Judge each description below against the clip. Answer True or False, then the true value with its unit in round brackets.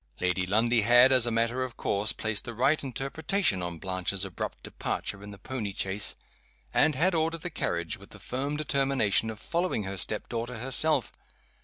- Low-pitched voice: True (115 Hz)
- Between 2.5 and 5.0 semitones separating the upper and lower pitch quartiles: False (5.4 semitones)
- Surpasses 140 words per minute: True (180 wpm)